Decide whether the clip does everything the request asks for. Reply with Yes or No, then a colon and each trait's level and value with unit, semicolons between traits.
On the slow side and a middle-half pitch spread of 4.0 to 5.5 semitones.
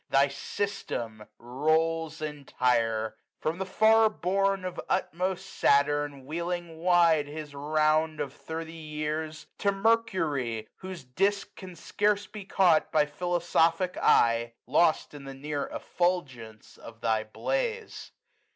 Yes: slow, 125 wpm; average, 4.7 semitones